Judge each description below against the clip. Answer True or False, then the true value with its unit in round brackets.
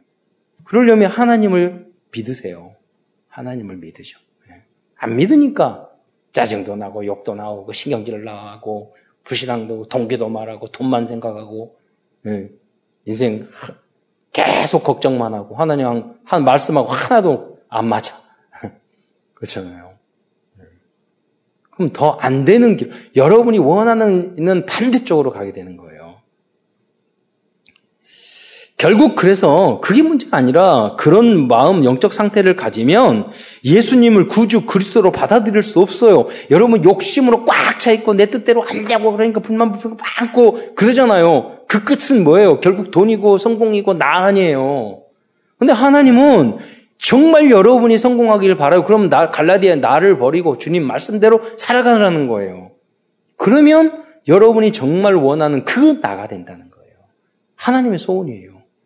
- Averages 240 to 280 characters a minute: False (290 characters per minute)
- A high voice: True (200 Hz)